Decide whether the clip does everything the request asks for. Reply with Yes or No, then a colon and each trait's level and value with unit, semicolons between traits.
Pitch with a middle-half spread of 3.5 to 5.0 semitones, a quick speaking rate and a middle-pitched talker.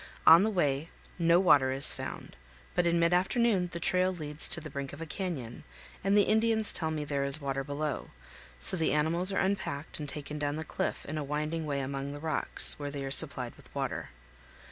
Yes: average, 3.8 semitones; fast, 210 wpm; medium, 155 Hz